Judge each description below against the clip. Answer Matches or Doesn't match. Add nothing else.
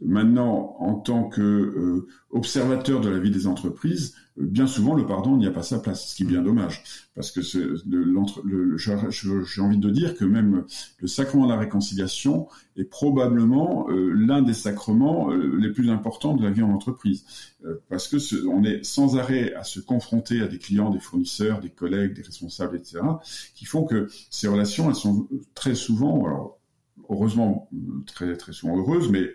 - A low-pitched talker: Matches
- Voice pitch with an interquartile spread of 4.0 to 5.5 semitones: Matches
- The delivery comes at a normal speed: Matches